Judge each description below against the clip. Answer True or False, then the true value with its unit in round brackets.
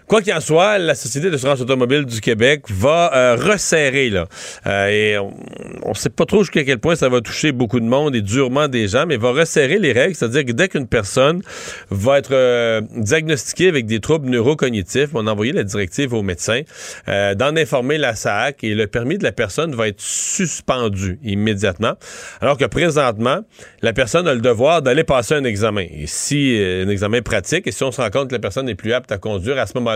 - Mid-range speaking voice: False (125 Hz)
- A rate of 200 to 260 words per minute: True (220 wpm)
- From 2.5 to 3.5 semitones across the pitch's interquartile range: False (5.1 semitones)